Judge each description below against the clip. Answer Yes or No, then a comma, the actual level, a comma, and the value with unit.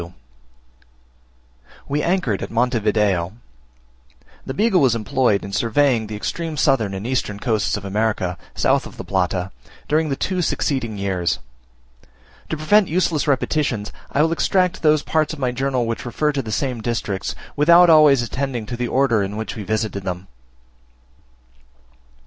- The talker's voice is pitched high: No, low, 120 Hz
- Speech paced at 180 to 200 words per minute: No, average, 155 wpm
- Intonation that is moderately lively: No, wide, 6.1 semitones